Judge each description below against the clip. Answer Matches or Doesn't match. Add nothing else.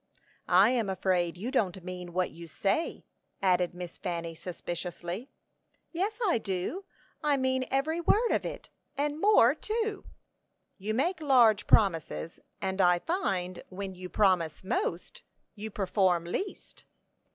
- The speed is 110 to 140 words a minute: Matches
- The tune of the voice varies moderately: Doesn't match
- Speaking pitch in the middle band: Doesn't match